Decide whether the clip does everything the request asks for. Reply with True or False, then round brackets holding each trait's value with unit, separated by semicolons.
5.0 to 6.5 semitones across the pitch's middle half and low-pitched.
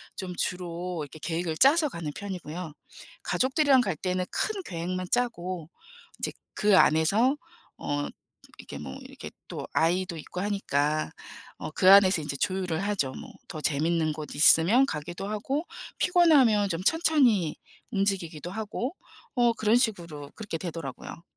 False (5.3 semitones; 185 Hz)